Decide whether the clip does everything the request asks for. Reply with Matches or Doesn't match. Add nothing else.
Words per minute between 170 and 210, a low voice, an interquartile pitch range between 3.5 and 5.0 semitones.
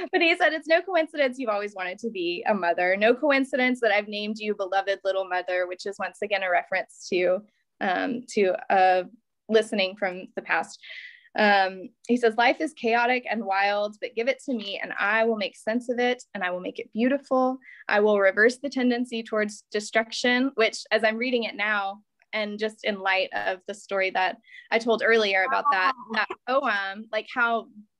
Doesn't match